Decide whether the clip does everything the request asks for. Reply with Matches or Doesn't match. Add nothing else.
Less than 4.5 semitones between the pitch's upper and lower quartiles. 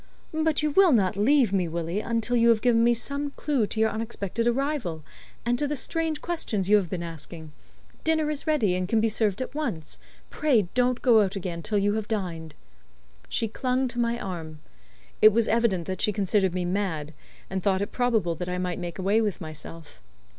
Doesn't match